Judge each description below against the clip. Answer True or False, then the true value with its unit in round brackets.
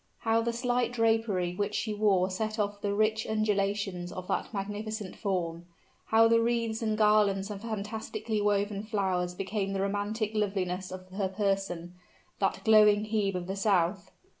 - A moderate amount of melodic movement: False (2.1 semitones)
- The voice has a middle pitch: False (205 Hz)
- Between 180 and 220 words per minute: False (160 wpm)